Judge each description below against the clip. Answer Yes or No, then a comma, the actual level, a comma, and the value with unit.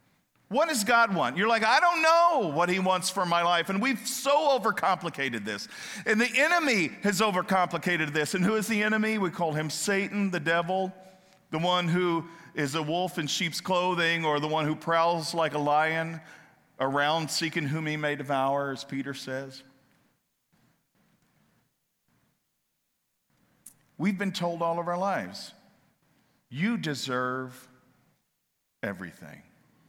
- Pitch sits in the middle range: Yes, medium, 170 Hz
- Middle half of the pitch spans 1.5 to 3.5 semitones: No, average, 4.6 semitones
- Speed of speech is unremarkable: Yes, average, 145 wpm